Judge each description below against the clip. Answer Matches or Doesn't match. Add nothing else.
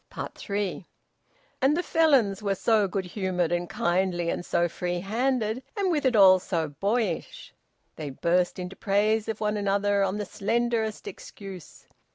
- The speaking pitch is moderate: Doesn't match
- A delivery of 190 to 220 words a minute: Doesn't match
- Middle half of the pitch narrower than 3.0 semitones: Doesn't match